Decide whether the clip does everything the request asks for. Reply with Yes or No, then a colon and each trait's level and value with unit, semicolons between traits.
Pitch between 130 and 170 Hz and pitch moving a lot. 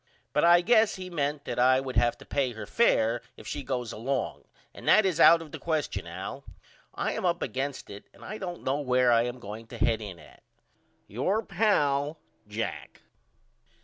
Yes: low, 135 Hz; wide, 6.4 semitones